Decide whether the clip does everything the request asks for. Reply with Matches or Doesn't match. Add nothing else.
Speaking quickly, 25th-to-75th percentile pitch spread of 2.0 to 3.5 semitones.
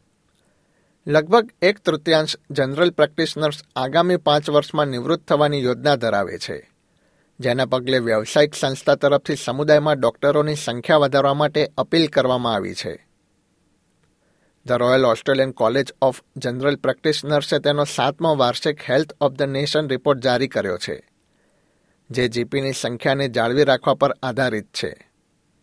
Doesn't match